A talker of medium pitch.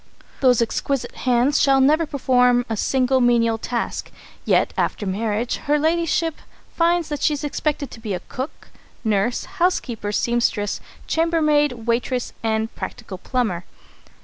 No: very high, 250 Hz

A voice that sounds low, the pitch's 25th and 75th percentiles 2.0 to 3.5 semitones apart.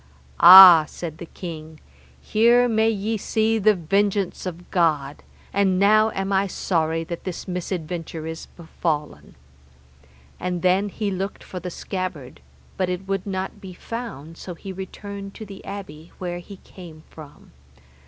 No: medium, 185 Hz; average, 3.2 semitones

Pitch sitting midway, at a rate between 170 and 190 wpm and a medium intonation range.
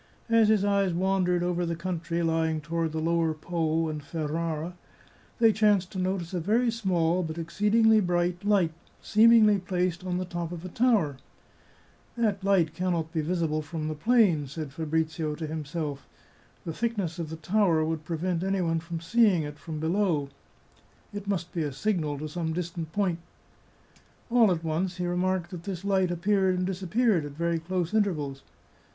Yes: medium, 175 Hz; average, 180 wpm; average, 3.1 semitones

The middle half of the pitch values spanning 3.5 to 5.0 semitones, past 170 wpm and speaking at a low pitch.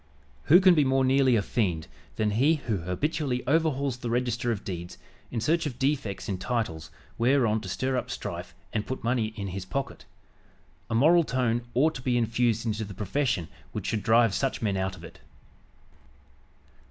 Yes: average, 4.2 semitones; average, 180 wpm; low, 120 Hz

